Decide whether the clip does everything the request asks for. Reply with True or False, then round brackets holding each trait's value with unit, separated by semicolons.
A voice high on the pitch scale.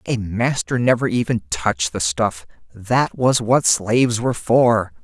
False (110 Hz)